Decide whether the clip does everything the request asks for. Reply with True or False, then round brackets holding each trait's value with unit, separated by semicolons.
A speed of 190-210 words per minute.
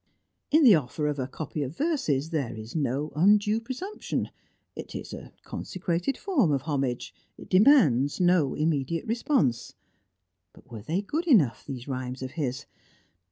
False (155 wpm)